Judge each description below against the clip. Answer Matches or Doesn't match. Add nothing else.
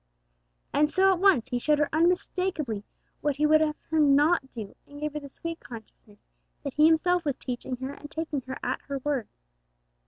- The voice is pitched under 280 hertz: Doesn't match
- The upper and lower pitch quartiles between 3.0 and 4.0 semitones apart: Matches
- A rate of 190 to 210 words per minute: Matches